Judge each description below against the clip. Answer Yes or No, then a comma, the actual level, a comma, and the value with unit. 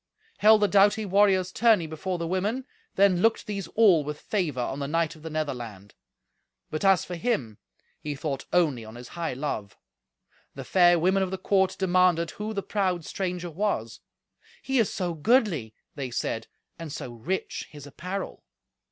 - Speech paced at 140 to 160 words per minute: No, average, 170 wpm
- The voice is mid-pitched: Yes, medium, 175 Hz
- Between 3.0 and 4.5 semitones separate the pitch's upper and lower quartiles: No, average, 4.9 semitones